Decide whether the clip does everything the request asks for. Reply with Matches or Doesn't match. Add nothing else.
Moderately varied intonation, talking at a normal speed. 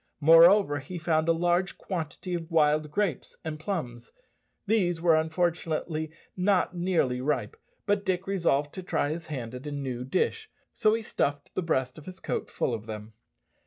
Matches